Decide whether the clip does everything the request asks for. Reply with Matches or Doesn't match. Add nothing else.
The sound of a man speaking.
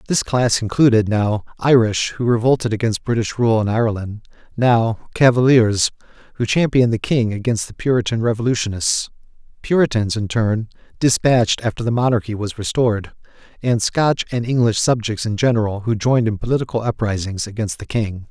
Matches